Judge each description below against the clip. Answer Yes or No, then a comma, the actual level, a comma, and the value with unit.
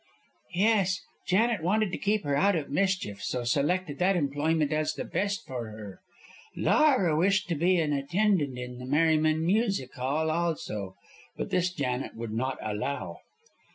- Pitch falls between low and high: Yes, medium, 155 Hz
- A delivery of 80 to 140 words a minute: No, average, 155 wpm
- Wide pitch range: Yes, wide, 5.9 semitones